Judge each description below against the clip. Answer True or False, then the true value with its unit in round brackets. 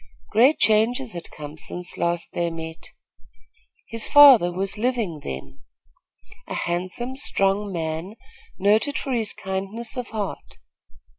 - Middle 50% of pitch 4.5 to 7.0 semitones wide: True (5.2 semitones)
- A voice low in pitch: False (195 Hz)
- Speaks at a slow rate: True (125 wpm)